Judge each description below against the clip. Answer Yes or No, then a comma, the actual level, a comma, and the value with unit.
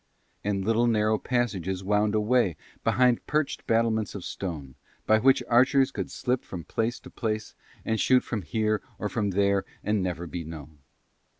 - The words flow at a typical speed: Yes, average, 165 wpm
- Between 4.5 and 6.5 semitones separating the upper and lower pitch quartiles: No, average, 3.7 semitones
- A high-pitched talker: No, low, 110 Hz